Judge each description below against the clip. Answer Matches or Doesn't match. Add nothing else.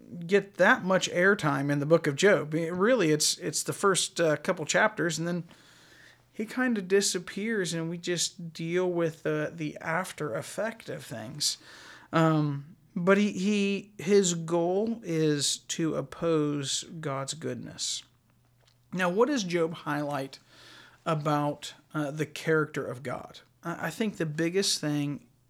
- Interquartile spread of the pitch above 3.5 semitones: Matches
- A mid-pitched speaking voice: Matches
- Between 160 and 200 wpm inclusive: Doesn't match